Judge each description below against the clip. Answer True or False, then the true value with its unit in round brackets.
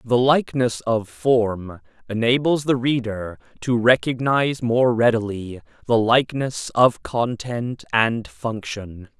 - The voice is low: True (120 Hz)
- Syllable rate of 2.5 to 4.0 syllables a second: True (3.7 syllables/s)